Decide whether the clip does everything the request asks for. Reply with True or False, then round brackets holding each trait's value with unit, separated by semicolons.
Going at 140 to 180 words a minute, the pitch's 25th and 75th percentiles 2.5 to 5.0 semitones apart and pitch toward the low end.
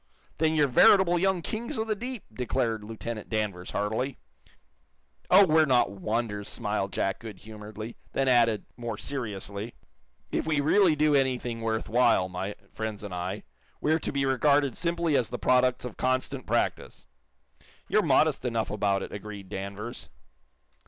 False (150 wpm; 5.5 semitones; 120 Hz)